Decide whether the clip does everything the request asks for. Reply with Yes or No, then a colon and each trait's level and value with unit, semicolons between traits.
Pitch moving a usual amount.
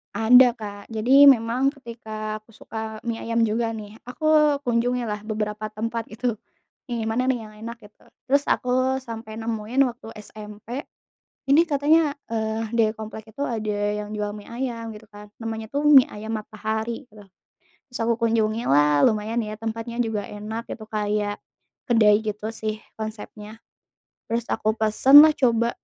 No: narrow, 2.0 semitones